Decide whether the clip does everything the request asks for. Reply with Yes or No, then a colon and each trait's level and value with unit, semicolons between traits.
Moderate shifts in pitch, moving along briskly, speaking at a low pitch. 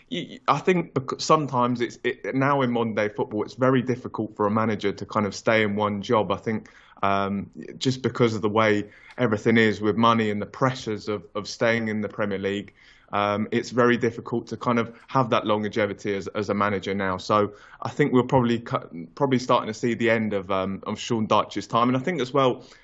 Yes: average, 3.1 semitones; fast, 220 wpm; low, 110 Hz